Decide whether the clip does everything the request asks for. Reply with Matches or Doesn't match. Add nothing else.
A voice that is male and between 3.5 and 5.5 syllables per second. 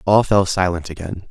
Matches